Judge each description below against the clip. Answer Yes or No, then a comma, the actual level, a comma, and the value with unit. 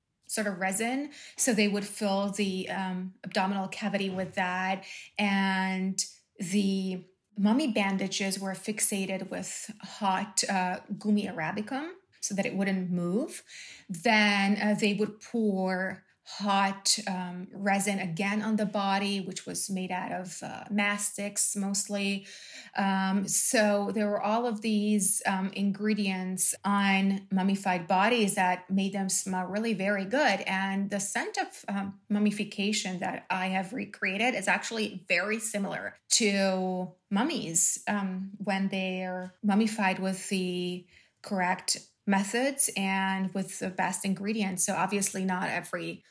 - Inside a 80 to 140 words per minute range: Yes, slow, 135 wpm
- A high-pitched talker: Yes, high, 195 Hz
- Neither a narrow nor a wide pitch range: No, narrow, 1.6 semitones